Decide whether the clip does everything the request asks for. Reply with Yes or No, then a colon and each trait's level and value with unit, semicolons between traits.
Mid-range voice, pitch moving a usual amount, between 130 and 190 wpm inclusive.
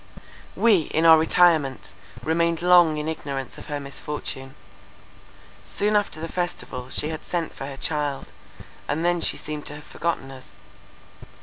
Yes: medium, 155 Hz; average, 3.1 semitones; average, 150 wpm